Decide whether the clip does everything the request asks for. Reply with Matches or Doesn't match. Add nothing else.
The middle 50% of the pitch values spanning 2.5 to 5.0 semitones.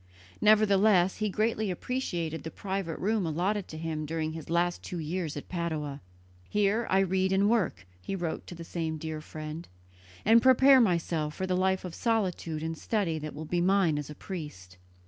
Matches